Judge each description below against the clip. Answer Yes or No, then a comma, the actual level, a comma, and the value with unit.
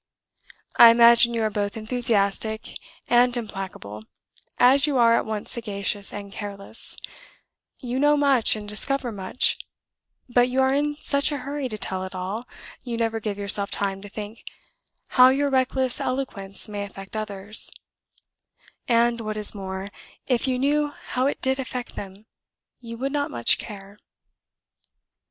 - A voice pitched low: No, high, 230 Hz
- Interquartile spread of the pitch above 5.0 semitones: No, average, 4.2 semitones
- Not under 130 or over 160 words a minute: Yes, average, 150 wpm